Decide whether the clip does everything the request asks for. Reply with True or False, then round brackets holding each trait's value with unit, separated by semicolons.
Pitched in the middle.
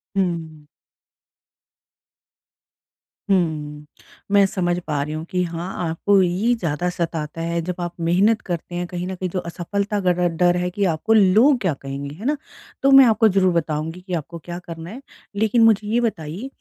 True (180 Hz)